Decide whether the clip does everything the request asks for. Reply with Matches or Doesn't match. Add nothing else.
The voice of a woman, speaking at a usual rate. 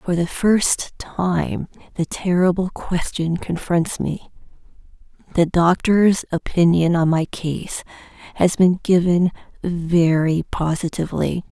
Doesn't match